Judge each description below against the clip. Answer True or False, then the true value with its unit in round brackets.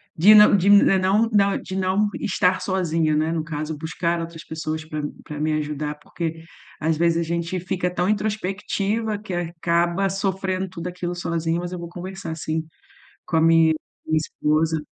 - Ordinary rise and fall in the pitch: True (3.0 semitones)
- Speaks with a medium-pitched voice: True (170 Hz)